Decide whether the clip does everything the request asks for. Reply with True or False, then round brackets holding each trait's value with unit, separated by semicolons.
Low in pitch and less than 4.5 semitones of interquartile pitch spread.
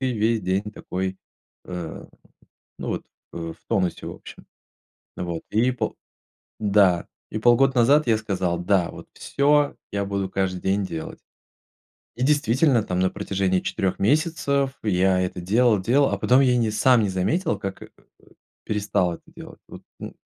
False (105 Hz; 5.0 semitones)